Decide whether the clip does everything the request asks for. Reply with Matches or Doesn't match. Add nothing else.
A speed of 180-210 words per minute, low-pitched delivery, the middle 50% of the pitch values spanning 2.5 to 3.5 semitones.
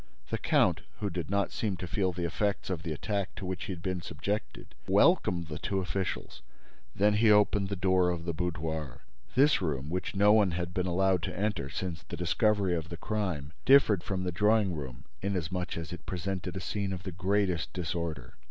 Matches